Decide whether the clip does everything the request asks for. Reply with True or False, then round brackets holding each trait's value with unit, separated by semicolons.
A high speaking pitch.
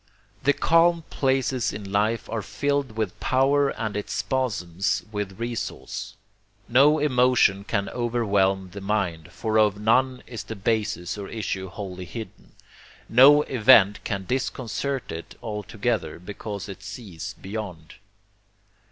False (110 Hz)